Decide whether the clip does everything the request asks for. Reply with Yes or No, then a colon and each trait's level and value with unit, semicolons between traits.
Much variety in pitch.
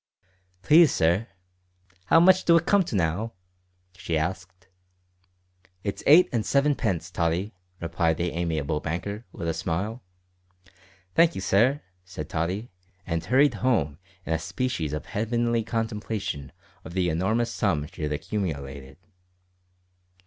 Yes: wide, 6.1 semitones